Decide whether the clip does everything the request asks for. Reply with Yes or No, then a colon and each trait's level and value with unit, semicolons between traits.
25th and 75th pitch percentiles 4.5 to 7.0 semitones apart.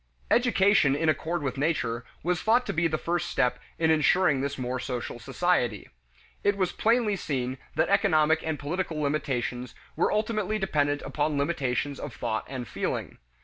Yes: average, 5.0 semitones